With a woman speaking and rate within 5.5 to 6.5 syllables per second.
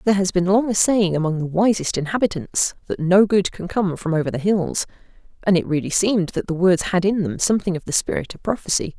Yes: female; 6.0 syllables/s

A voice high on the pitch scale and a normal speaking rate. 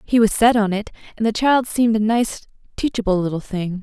No: high, 215 Hz; fast, 220 wpm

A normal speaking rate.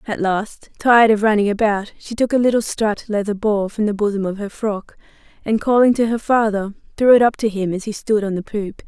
No: fast, 235 wpm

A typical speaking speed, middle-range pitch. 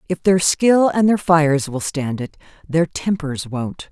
Yes: average, 185 wpm; medium, 160 Hz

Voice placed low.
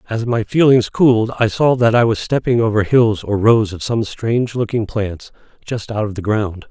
Yes: low, 110 Hz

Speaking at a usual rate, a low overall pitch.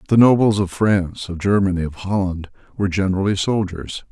Yes: average, 160 wpm; very low, 95 Hz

